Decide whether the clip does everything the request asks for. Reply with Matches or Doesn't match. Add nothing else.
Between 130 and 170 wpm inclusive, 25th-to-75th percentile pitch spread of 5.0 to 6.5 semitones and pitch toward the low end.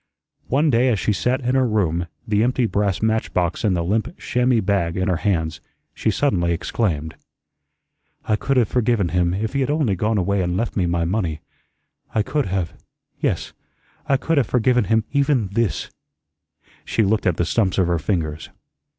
Doesn't match